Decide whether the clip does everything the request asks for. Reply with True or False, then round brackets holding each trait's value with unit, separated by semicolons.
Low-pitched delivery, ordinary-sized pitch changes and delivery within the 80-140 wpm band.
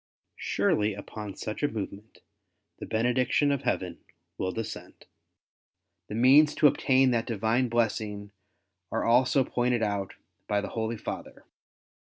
True (115 Hz; 3.5 semitones; 135 wpm)